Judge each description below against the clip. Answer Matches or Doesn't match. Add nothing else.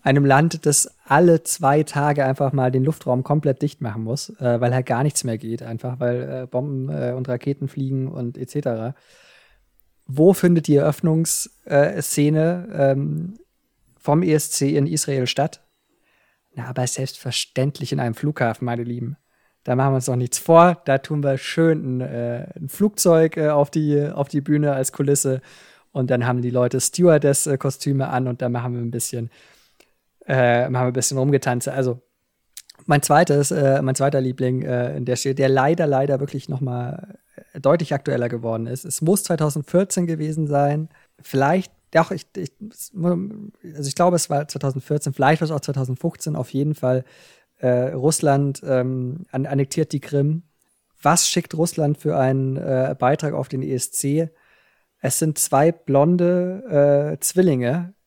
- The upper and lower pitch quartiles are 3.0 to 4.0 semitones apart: Matches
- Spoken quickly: Doesn't match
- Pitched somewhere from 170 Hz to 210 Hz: Doesn't match